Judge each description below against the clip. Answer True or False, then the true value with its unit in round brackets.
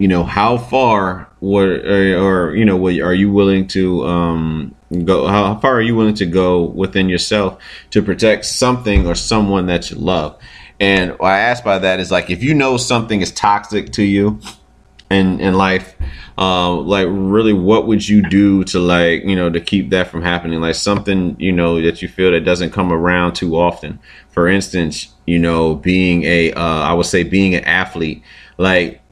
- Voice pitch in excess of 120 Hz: False (95 Hz)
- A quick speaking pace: False (195 wpm)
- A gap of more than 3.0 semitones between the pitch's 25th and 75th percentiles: False (2.5 semitones)